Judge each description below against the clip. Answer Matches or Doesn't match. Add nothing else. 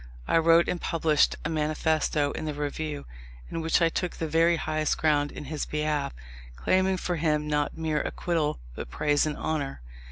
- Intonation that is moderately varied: Doesn't match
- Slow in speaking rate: Doesn't match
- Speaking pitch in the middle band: Matches